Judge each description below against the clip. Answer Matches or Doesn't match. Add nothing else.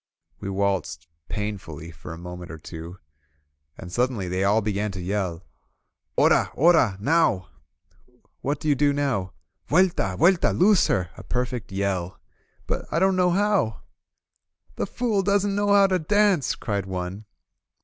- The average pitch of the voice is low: Matches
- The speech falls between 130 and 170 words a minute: Matches